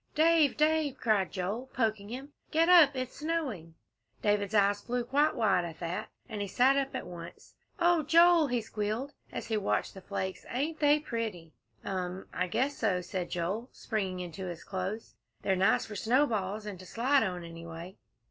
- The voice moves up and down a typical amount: No, wide, 6.7 semitones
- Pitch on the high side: Yes, high, 215 Hz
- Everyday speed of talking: Yes, average, 175 wpm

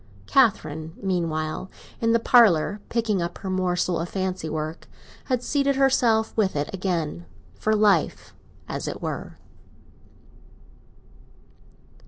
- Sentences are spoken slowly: Yes, slow, 110 wpm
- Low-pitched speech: No, medium, 185 Hz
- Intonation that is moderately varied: No, wide, 5.8 semitones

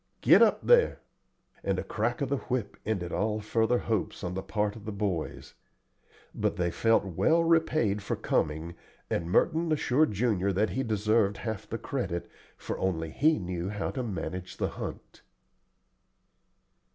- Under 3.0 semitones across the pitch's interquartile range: No, average, 5.0 semitones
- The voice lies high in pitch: No, low, 105 Hz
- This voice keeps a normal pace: Yes, average, 160 wpm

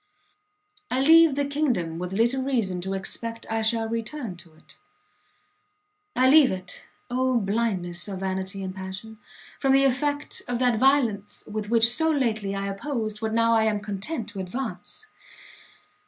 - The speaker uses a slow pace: No, average, 155 wpm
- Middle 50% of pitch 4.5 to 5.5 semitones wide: Yes, average, 5.0 semitones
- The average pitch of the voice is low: No, high, 225 Hz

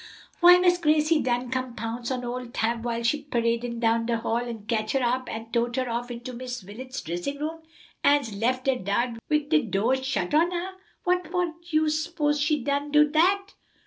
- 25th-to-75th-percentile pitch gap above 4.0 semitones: Yes, average, 4.4 semitones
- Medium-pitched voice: No, very high, 255 Hz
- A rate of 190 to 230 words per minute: Yes, average, 200 wpm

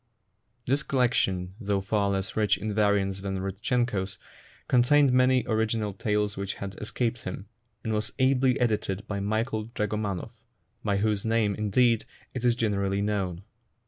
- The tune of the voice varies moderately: Yes, average, 3.0 semitones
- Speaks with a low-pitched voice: Yes, low, 105 Hz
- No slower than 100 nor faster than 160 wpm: Yes, average, 145 wpm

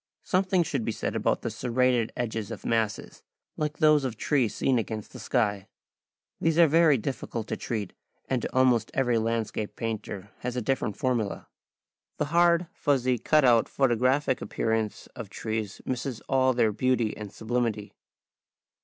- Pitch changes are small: No, average, 3.4 semitones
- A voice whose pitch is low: Yes, low, 120 Hz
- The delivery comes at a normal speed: Yes, average, 155 wpm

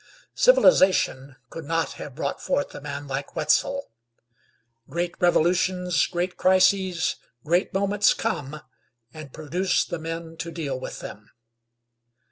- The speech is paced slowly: Yes, slow, 120 wpm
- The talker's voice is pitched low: No, medium, 170 Hz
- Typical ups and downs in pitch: Yes, average, 3.8 semitones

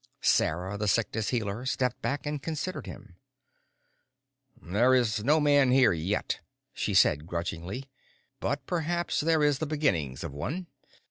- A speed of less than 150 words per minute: Yes, average, 140 wpm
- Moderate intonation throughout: No, wide, 6.9 semitones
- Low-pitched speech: Yes, low, 125 Hz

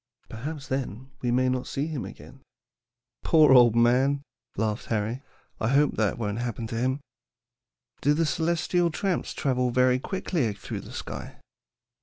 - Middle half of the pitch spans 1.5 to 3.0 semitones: No, average, 3.7 semitones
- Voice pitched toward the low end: Yes, low, 130 Hz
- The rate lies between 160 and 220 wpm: No, average, 150 wpm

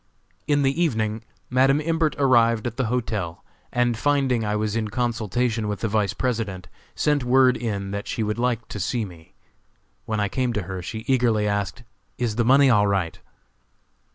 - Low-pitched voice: Yes, low, 115 Hz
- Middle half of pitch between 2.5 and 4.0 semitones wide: Yes, average, 3.3 semitones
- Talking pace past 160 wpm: Yes, average, 180 wpm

